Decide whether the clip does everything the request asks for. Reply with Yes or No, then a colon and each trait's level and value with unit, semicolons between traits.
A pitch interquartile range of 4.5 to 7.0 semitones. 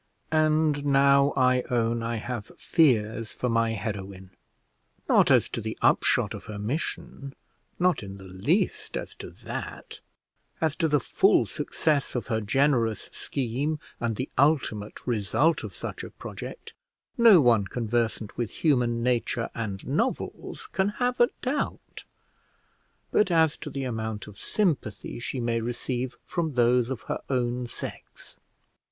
Yes: average, 5.0 semitones